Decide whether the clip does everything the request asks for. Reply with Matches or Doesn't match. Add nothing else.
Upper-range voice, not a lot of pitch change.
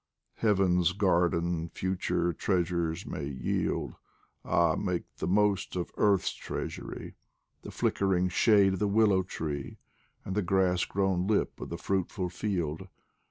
Doesn't match